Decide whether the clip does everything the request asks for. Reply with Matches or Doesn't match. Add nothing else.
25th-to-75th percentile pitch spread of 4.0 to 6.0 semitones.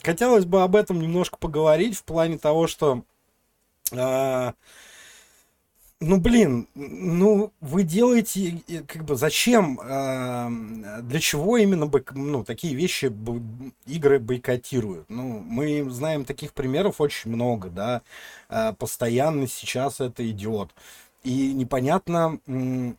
Matches